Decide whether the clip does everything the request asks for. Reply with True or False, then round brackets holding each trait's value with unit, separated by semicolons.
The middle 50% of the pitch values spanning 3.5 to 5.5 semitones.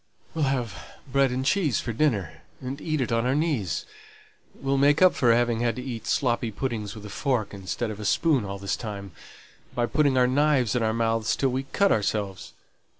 True (4.1 semitones)